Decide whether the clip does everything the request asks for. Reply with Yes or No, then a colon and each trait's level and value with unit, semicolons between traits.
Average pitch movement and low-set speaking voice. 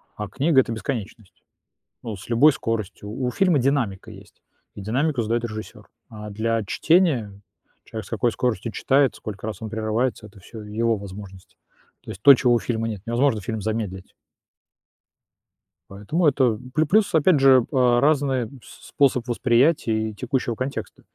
Yes: average, 3.9 semitones; low, 115 Hz